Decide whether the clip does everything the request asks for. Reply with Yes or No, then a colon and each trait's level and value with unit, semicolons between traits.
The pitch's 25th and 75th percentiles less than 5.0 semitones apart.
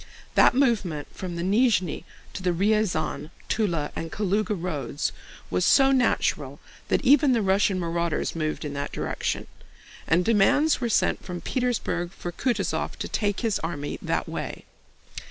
No: average, 5.3 semitones